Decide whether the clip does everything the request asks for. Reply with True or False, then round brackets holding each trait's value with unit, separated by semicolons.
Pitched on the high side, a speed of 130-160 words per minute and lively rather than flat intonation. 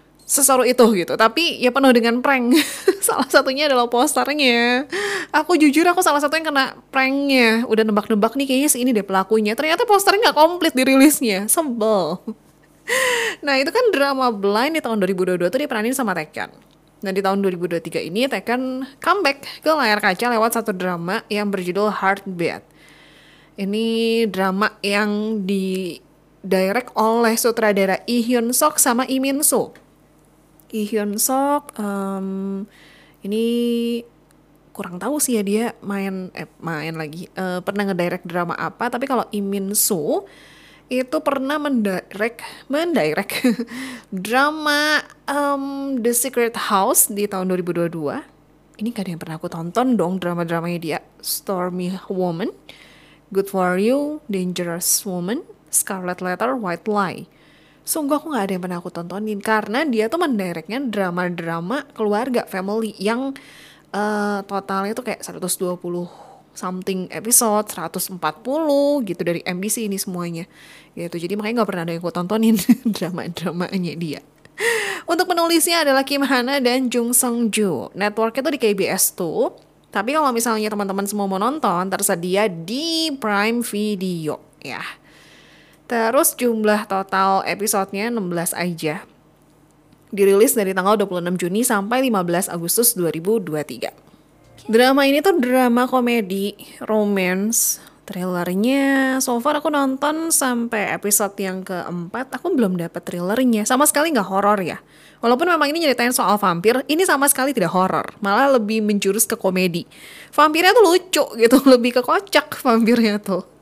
True (215 Hz; 135 wpm; 5.8 semitones)